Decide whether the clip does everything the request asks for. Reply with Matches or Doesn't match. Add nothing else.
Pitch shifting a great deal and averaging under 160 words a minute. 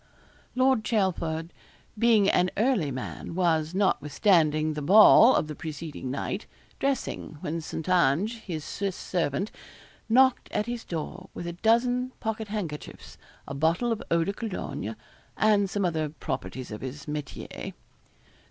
Matches